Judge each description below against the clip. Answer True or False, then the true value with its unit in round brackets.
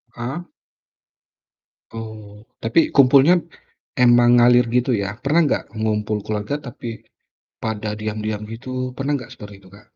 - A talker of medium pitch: False (115 Hz)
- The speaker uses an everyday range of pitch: True (3.1 semitones)